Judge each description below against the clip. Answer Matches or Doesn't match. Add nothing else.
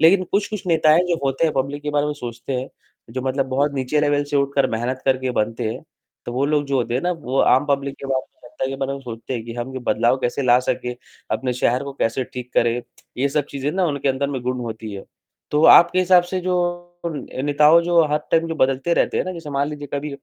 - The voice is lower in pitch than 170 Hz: Matches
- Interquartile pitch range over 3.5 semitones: Doesn't match